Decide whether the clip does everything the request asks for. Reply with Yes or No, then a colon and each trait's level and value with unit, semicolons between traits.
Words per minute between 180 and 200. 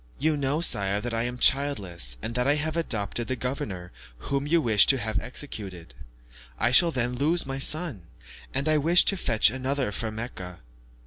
Yes: average, 185 wpm